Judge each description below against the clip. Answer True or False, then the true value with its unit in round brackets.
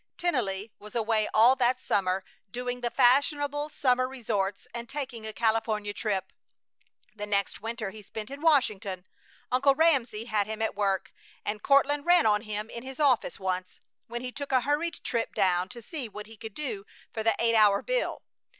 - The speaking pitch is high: True (230 Hz)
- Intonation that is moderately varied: True (4.1 semitones)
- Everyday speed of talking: True (180 wpm)